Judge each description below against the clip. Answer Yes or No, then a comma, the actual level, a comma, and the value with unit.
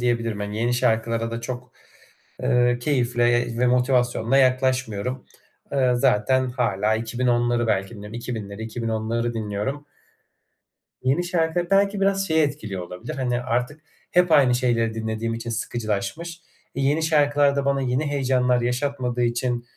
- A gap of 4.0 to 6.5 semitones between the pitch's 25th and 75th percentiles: No, average, 2.9 semitones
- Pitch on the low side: Yes, low, 125 Hz